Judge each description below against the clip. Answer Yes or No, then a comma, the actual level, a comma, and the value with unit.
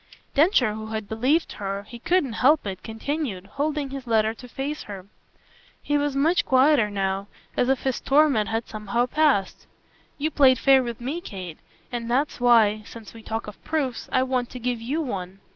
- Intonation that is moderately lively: Yes, average, 4.6 semitones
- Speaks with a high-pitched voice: Yes, high, 245 Hz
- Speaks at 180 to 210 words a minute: Yes, average, 185 wpm